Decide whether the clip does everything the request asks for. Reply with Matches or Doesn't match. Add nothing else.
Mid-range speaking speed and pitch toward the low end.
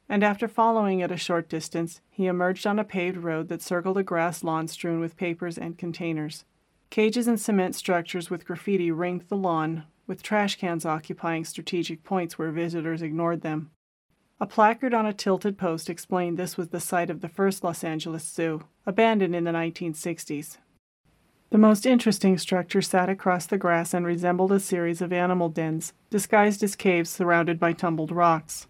Doesn't match